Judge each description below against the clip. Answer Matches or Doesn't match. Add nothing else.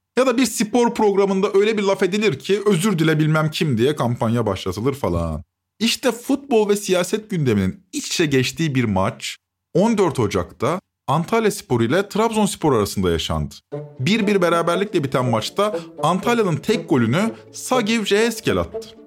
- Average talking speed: Doesn't match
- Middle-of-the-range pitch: Matches